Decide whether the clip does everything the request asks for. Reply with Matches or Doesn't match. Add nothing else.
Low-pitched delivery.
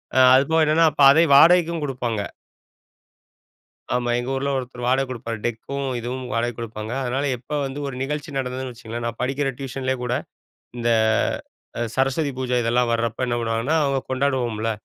Matches